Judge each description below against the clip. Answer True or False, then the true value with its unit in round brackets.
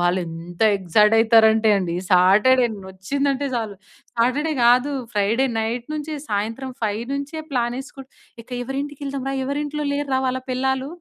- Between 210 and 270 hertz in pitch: True (245 Hz)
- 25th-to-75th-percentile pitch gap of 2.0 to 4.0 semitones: False (4.6 semitones)